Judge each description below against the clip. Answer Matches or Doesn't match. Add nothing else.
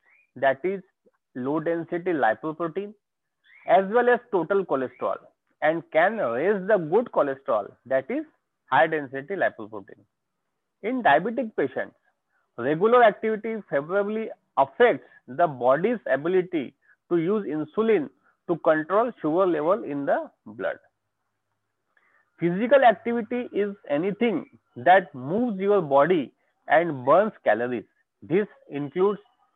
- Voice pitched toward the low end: Doesn't match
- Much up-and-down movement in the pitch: Matches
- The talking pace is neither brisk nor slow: Doesn't match